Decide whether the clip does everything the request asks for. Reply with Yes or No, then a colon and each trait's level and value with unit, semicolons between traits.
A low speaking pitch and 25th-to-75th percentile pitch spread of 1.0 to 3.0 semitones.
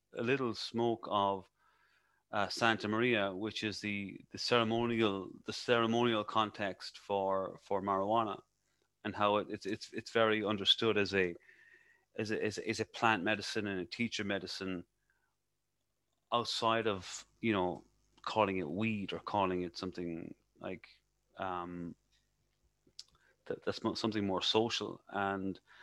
Yes: low, 105 Hz; average, 2.7 semitones